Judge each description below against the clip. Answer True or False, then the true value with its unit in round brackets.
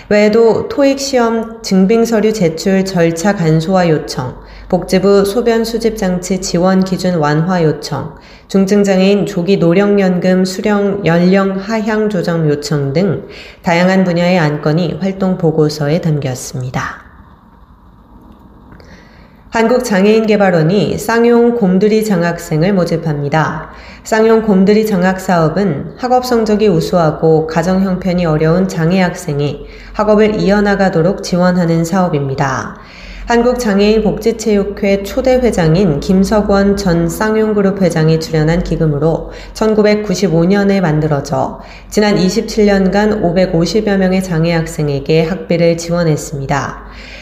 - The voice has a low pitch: False (185 Hz)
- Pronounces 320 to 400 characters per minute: False (270 characters per minute)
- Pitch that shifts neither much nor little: True (4.1 semitones)